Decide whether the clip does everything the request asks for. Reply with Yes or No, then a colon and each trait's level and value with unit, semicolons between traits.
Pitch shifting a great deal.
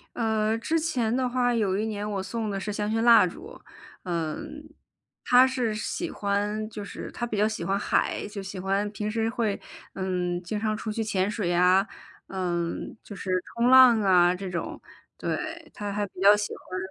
No: average, 3.0 semitones